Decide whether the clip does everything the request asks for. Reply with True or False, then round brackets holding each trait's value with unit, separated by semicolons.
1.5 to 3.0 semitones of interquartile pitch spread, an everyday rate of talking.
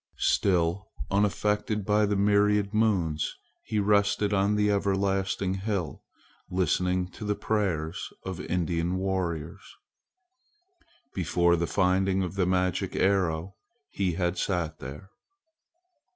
False (2.6 semitones; 110 wpm)